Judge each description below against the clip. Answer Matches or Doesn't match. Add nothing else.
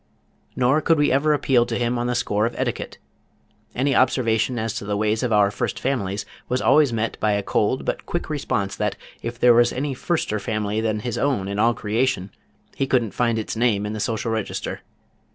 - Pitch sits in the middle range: Doesn't match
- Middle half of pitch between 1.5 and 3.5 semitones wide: Matches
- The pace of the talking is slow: Doesn't match